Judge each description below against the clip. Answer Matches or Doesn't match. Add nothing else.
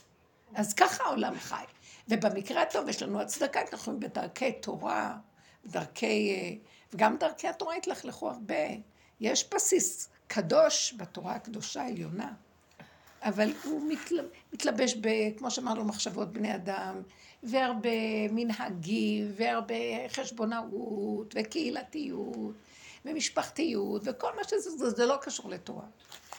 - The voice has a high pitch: Matches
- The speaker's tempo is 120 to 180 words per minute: Doesn't match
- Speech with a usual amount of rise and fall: Doesn't match